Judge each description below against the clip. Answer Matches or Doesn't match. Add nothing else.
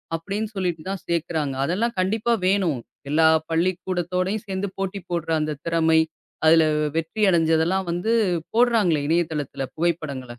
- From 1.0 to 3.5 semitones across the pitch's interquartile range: Matches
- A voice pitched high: Doesn't match